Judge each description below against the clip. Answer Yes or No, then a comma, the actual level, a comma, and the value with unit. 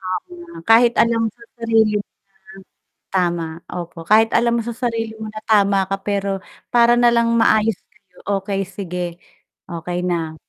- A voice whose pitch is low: No, high, 210 Hz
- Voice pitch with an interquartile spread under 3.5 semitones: No, average, 3.9 semitones